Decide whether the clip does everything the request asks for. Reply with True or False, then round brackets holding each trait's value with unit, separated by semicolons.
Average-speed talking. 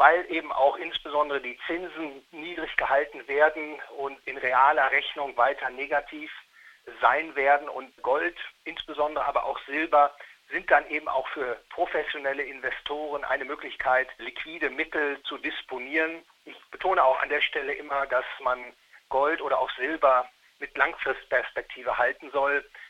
True (140 wpm)